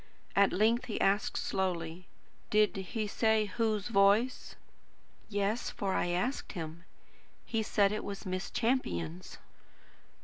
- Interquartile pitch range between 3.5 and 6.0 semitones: No, average, 3.1 semitones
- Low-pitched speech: No, high, 200 Hz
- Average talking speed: No, slow, 125 wpm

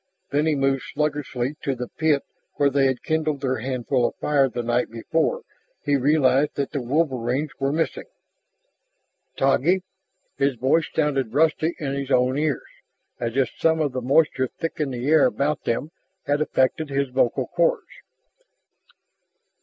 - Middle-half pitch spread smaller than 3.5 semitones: Yes, average, 2.8 semitones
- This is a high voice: No, medium, 140 Hz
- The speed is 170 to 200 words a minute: No, average, 160 wpm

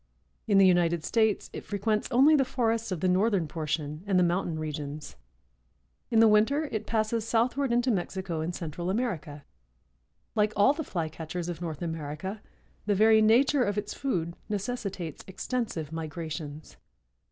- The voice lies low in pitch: No, high, 190 Hz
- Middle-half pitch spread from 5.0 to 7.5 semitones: Yes, wide, 5.5 semitones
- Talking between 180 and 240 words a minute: No, average, 155 wpm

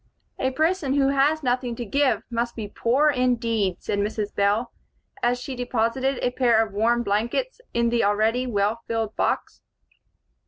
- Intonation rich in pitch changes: No, average, 2.9 semitones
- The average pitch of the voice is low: No, high, 235 Hz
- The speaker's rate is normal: Yes, average, 160 wpm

